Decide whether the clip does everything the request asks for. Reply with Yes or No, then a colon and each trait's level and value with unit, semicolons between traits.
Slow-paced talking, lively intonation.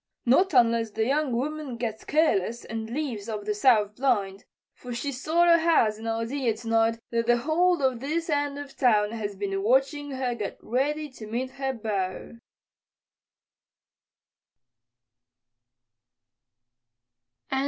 No: slow, 130 wpm; average, 4.3 semitones